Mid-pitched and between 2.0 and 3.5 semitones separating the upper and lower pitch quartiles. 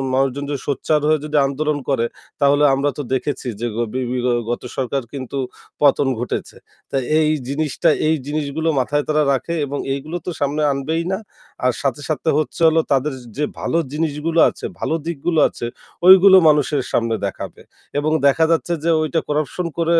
Yes: medium, 145 Hz; narrow, 2.5 semitones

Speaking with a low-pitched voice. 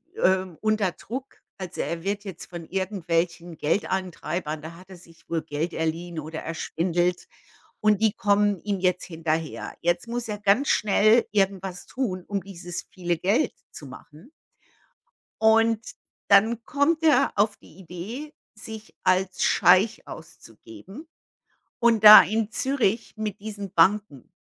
No: high, 190 Hz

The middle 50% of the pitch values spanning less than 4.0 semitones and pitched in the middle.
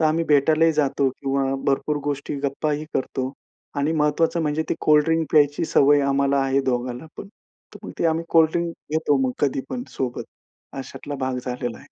Yes: average, 2.7 semitones; medium, 145 Hz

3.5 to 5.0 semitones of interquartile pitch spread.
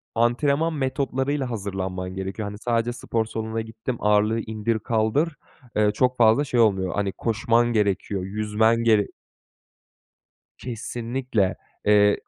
No: average, 2.7 semitones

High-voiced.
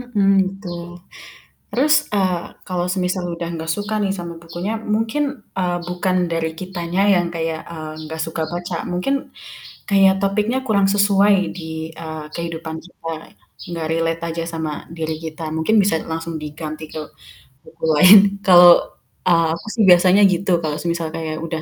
No: medium, 175 Hz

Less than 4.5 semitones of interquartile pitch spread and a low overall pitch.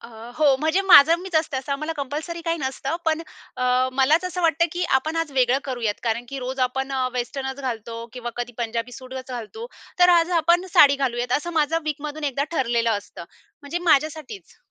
No: average, 4.1 semitones; very high, 275 Hz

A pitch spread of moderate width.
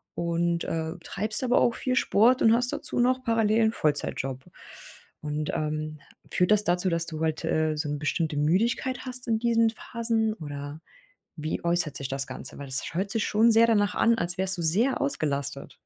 No: wide, 6.8 semitones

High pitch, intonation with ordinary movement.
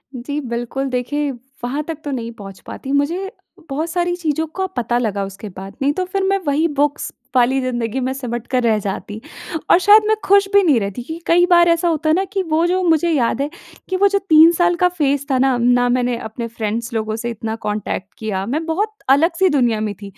No: very high, 275 Hz; wide, 6.2 semitones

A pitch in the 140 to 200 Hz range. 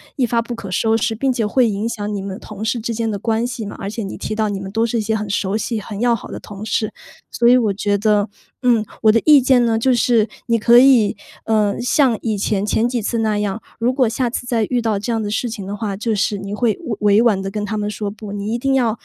No: high, 220 Hz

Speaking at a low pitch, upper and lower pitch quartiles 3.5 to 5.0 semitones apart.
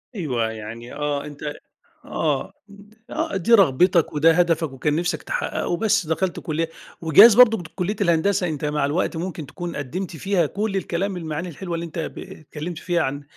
No: medium, 165 Hz; average, 4.0 semitones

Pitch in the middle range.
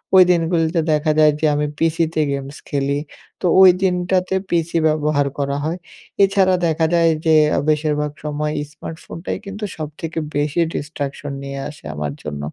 Yes: medium, 155 Hz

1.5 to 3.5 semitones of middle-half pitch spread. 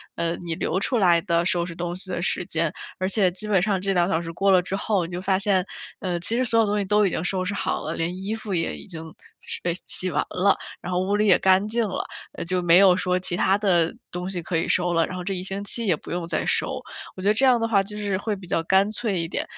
Yes: narrow, 2.5 semitones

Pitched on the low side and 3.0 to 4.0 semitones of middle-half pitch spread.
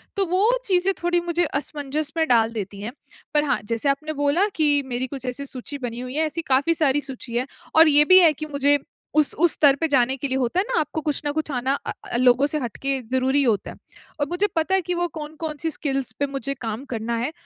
No: very high, 285 Hz; average, 3.6 semitones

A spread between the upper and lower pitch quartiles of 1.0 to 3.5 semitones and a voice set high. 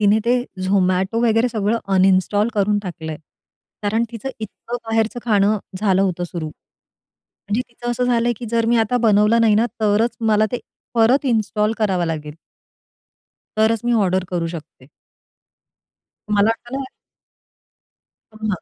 Yes: average, 3.2 semitones; high, 215 Hz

